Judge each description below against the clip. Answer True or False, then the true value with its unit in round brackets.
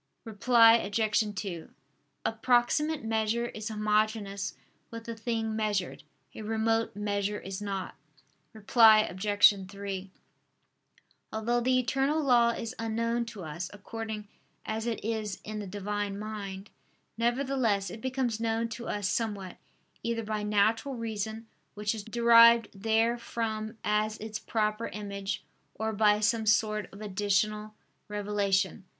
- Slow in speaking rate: True (130 wpm)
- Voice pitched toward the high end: True (215 Hz)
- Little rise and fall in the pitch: True (1.9 semitones)